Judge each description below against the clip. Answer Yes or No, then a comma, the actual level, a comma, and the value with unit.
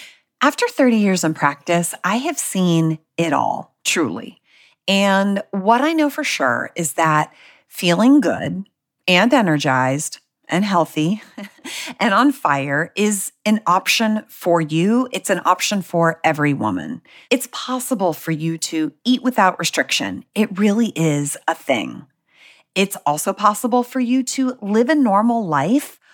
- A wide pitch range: Yes, wide, 6.8 semitones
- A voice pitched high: Yes, high, 195 Hz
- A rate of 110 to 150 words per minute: Yes, average, 140 wpm